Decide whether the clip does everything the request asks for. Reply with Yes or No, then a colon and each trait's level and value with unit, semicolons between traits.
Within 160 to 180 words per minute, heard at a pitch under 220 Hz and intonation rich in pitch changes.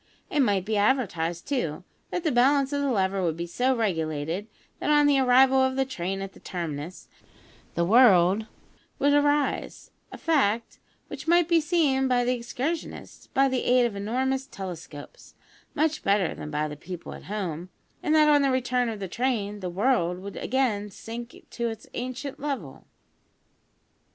No: average, 170 wpm; high, 235 Hz; wide, 6.3 semitones